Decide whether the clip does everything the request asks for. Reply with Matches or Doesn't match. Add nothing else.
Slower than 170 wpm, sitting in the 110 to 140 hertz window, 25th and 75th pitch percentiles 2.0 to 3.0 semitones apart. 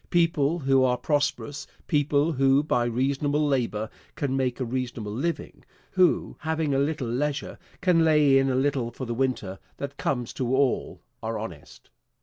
Matches